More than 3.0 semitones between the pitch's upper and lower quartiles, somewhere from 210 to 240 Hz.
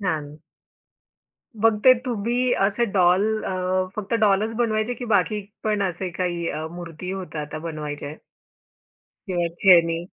No: average, 4.5 semitones; high, 190 Hz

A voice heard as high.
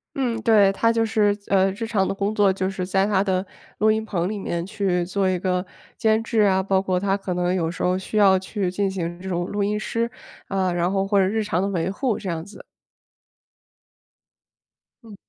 Yes: high, 195 Hz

